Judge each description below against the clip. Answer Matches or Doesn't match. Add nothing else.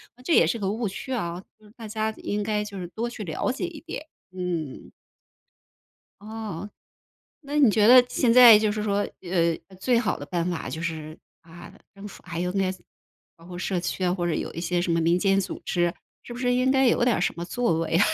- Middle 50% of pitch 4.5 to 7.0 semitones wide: Matches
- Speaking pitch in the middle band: Doesn't match